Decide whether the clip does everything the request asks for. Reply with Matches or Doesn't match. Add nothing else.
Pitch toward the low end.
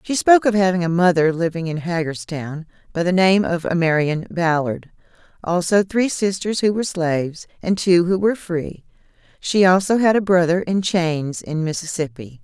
Doesn't match